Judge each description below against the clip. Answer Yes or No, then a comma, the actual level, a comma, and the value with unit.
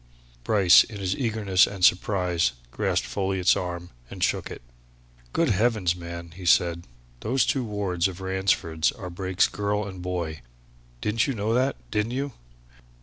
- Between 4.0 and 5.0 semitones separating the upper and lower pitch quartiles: No, average, 3.2 semitones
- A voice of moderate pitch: No, very low, 95 Hz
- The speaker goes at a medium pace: Yes, average, 150 wpm